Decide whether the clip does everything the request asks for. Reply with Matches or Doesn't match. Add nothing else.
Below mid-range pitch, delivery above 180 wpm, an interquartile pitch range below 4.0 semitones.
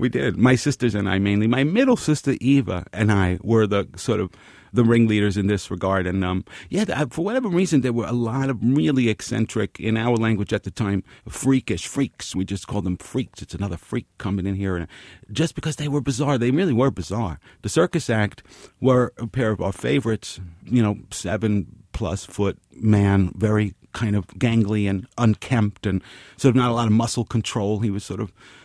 Doesn't match